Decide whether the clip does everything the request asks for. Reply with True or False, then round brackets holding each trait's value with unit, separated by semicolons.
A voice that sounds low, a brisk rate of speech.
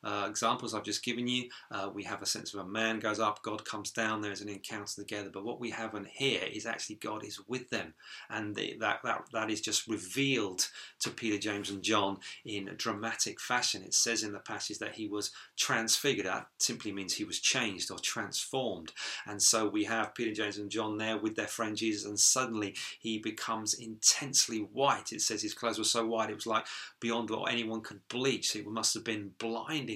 True (110 Hz; 220 wpm)